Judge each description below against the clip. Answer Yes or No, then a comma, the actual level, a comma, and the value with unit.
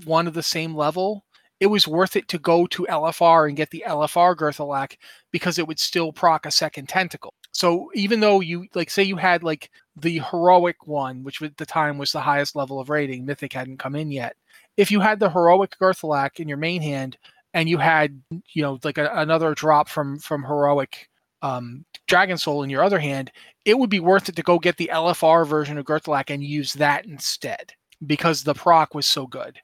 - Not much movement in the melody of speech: No, average, 3.0 semitones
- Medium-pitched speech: Yes, medium, 160 Hz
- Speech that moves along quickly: Yes, fast, 215 wpm